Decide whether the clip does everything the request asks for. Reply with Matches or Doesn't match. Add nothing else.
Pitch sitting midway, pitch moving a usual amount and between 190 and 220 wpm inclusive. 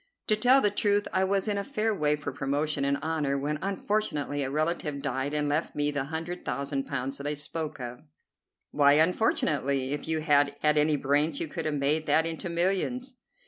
Matches